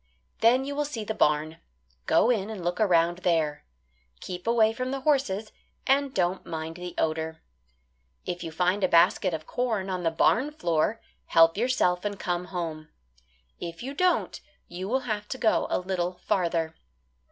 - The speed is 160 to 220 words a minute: Yes, average, 170 wpm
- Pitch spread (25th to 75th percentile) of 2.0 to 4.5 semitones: No, wide, 5.4 semitones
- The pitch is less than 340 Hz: Yes, medium, 185 Hz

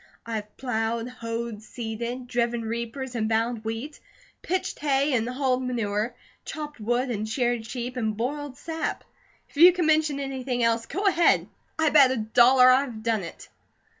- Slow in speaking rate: No, average, 165 wpm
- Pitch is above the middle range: Yes, high, 245 Hz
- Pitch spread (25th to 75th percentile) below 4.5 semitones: Yes, average, 3.2 semitones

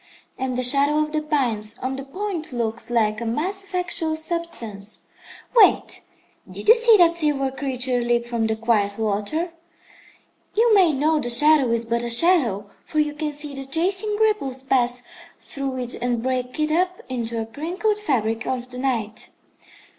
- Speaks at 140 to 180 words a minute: Yes, average, 175 wpm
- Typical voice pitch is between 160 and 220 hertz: No, very high, 265 Hz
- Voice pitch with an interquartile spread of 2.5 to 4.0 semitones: No, average, 5.2 semitones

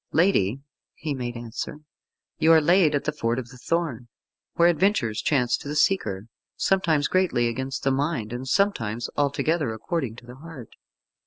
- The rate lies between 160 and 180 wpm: Yes, average, 165 wpm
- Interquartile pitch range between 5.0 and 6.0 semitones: Yes, wide, 5.4 semitones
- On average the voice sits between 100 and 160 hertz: Yes, medium, 140 Hz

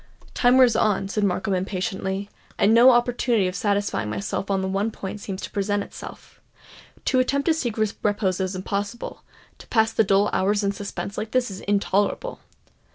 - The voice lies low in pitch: No, high, 205 Hz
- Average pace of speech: Yes, average, 175 wpm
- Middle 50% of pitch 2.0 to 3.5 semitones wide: Yes, narrow, 2.6 semitones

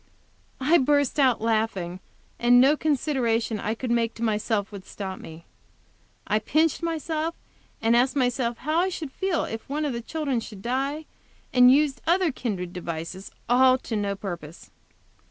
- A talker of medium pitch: No, high, 245 Hz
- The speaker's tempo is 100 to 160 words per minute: Yes, average, 155 wpm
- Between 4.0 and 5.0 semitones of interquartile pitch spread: No, wide, 5.4 semitones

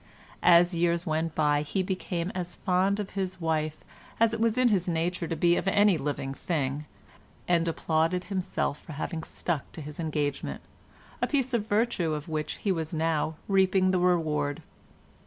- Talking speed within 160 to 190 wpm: Yes, average, 170 wpm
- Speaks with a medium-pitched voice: Yes, medium, 170 Hz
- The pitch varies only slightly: No, average, 3.2 semitones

